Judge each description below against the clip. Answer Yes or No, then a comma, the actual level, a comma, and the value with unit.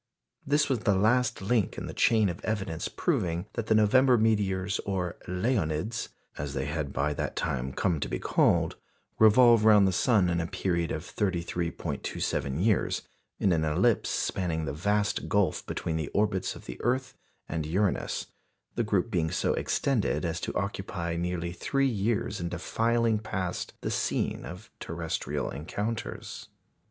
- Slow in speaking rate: No, average, 160 wpm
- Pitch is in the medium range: No, very low, 95 Hz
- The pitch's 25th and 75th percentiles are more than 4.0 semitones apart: Yes, average, 4.5 semitones